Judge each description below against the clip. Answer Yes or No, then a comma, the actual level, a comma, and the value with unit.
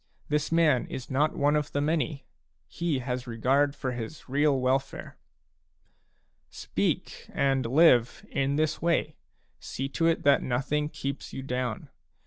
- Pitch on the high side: No, medium, 140 Hz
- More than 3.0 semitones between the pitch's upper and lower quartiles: No, narrow, 2.6 semitones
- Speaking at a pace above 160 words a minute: No, average, 140 wpm